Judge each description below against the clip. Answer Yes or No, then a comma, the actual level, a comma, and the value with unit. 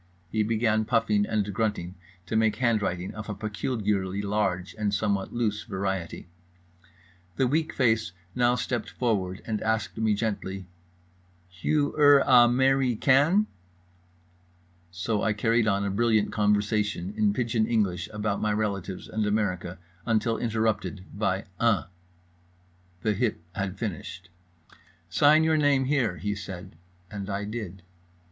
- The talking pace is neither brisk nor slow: No, slow, 130 wpm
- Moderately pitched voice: No, low, 105 Hz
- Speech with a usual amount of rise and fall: Yes, average, 3.0 semitones